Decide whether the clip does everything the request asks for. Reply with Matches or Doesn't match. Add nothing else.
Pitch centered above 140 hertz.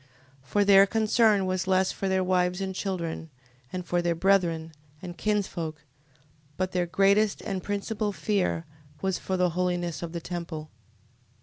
Matches